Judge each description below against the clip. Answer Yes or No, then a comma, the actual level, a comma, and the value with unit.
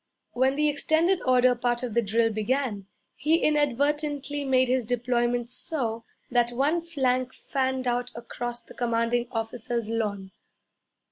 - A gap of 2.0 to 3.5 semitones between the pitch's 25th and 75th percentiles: Yes, average, 2.8 semitones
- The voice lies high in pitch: Yes, high, 245 Hz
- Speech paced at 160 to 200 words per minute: No, slow, 135 wpm